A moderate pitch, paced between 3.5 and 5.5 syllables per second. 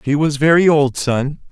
Yes: medium, 145 Hz; 4.5 syllables/s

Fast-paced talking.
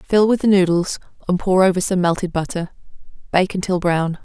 No: average, 185 wpm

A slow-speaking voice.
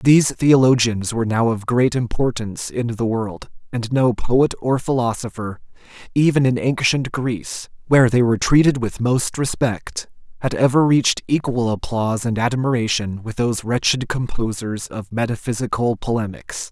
No: average, 145 wpm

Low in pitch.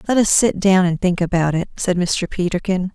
No: medium, 185 Hz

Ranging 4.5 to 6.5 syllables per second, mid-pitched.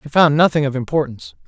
No: 7.0 syllables/s; medium, 145 Hz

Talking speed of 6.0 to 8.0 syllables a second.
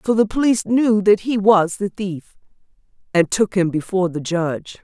No: 5.1 syllables/s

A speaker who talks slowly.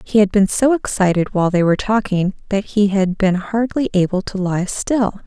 No: fast, 205 wpm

